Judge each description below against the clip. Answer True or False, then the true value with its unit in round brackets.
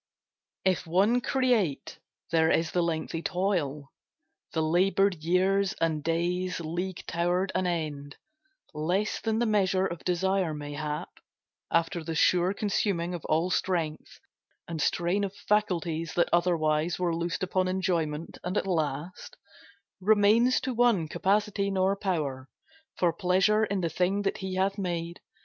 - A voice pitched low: False (180 Hz)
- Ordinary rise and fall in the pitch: True (3.0 semitones)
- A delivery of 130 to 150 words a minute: True (140 wpm)